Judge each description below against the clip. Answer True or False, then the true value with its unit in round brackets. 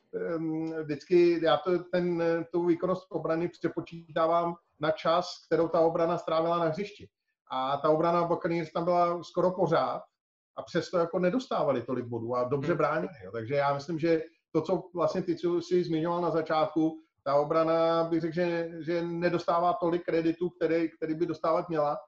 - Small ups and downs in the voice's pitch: True (1.5 semitones)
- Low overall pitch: False (165 Hz)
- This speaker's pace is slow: False (165 wpm)